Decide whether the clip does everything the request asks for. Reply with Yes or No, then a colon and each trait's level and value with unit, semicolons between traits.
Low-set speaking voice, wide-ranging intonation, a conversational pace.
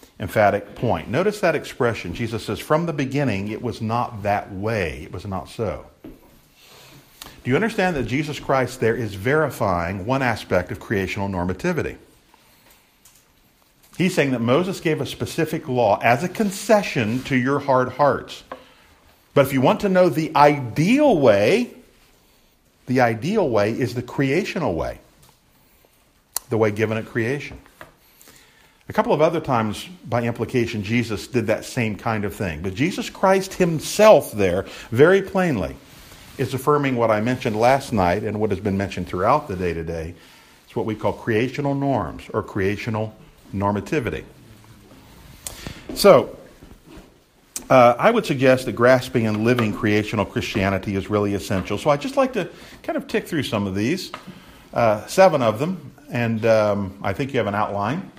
Yes: low, 120 Hz; wide, 6.1 semitones; average, 160 wpm